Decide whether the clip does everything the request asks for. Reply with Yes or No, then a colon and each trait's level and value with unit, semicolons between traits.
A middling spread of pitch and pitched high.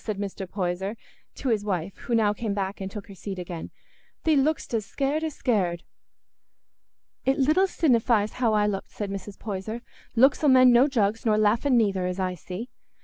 Yes: average, 4.4 semitones; high, 215 Hz